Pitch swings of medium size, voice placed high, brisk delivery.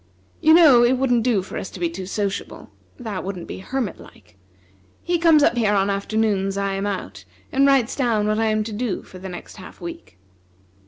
Yes: average, 4.2 semitones; high, 210 Hz; fast, 215 wpm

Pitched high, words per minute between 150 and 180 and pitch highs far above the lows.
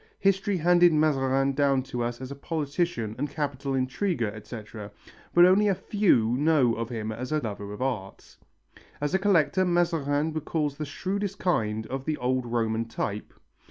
No: medium, 140 Hz; average, 160 wpm; wide, 6.0 semitones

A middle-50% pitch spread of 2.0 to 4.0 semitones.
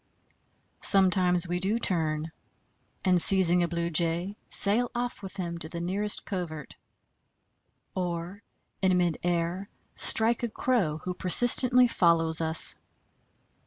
Yes: average, 2.9 semitones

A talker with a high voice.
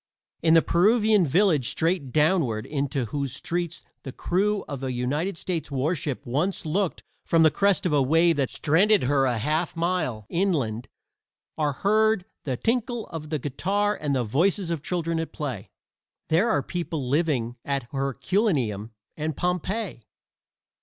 No: medium, 160 Hz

